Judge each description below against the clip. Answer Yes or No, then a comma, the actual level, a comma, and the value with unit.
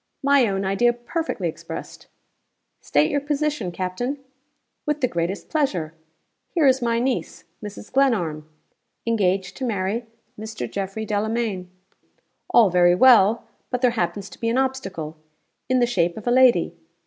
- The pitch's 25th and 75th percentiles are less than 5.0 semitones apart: No, wide, 5.6 semitones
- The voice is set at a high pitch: Yes, high, 220 Hz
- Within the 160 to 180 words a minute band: No, average, 145 wpm